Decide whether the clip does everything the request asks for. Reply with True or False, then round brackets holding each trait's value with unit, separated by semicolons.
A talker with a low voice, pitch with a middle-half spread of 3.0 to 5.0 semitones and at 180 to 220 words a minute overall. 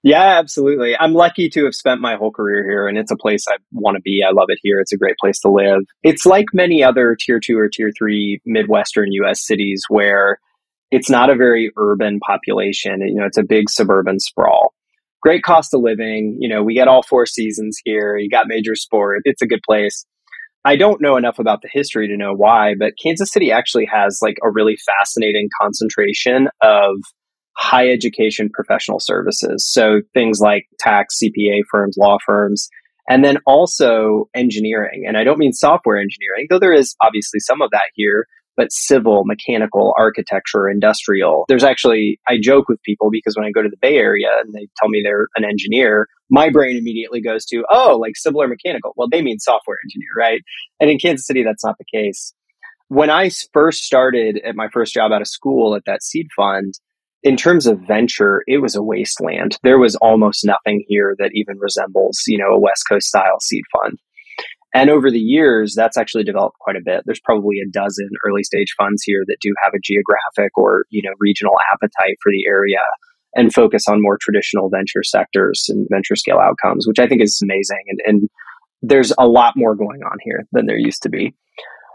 True (110 Hz; 4.0 semitones; 200 wpm)